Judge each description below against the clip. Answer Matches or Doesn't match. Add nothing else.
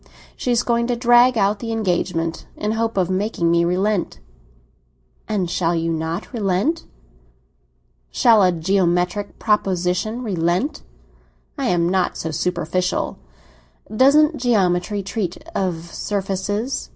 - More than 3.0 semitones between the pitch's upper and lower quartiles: Matches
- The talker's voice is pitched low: Doesn't match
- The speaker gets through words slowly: Matches